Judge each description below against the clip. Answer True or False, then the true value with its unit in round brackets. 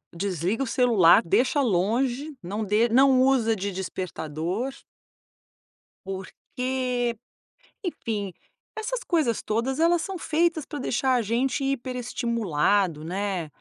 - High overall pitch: True (235 Hz)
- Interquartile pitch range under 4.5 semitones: False (5.5 semitones)